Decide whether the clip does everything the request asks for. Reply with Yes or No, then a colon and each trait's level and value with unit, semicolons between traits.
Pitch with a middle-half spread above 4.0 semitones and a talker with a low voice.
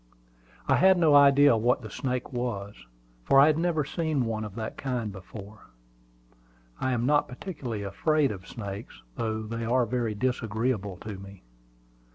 Yes: average, 4.5 semitones; low, 120 Hz